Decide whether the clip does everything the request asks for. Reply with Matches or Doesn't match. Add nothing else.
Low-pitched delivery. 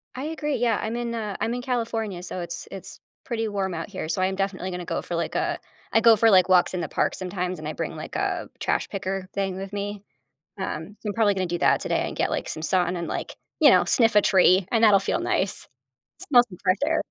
Doesn't match